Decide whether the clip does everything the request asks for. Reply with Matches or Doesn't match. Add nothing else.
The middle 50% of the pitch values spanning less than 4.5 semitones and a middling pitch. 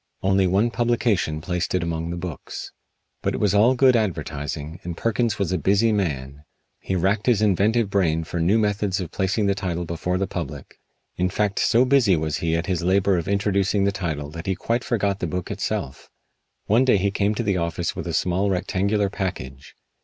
Doesn't match